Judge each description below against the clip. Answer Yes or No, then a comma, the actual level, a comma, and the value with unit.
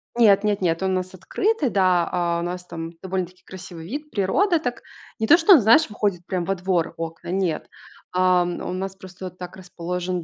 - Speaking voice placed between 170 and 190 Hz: Yes, medium, 185 Hz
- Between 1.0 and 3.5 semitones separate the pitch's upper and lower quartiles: Yes, narrow, 2.4 semitones